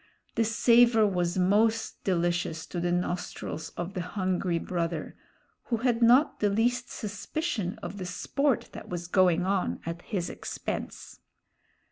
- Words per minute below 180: Yes, average, 140 wpm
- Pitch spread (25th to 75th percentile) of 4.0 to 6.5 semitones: Yes, average, 4.4 semitones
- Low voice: No, high, 190 Hz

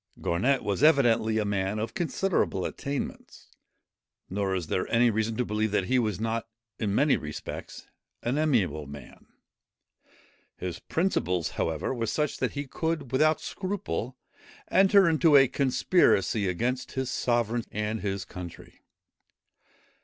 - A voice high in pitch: No, low, 115 Hz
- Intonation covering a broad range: Yes, wide, 6.1 semitones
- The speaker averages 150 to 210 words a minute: No, slow, 135 wpm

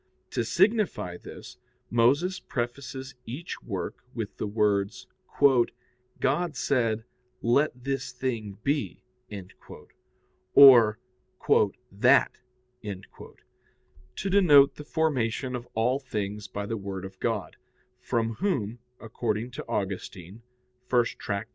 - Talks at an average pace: No, slow, 100 wpm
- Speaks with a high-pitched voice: No, low, 120 Hz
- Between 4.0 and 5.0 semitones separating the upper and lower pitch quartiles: Yes, average, 4.7 semitones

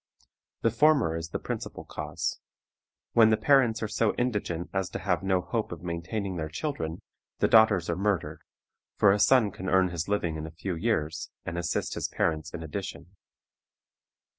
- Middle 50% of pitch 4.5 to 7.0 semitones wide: Yes, average, 4.8 semitones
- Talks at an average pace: Yes, average, 175 wpm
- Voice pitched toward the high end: No, very low, 95 Hz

